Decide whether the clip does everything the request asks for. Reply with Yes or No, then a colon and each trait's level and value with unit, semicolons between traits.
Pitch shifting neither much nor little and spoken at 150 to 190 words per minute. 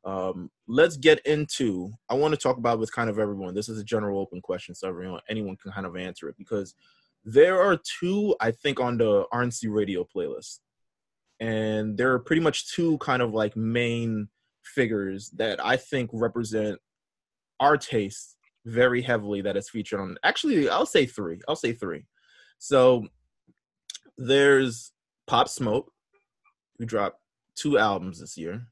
Yes: average, 4.1 semitones; average, 165 wpm